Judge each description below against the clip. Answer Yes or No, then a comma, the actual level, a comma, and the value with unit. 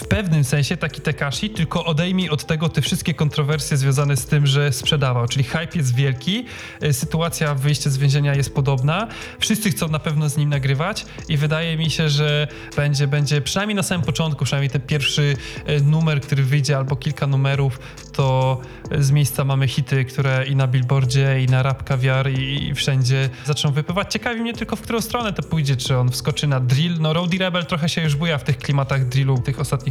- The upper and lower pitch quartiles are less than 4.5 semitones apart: Yes, average, 2.8 semitones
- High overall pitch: No, medium, 145 Hz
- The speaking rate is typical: No, fast, 200 wpm